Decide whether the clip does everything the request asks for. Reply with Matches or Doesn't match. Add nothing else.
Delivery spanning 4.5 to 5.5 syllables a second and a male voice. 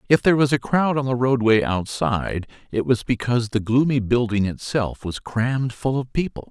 Matches